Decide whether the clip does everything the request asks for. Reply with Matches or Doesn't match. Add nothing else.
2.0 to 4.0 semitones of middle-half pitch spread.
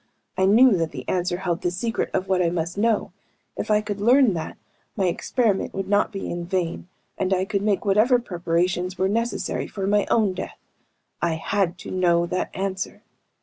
Matches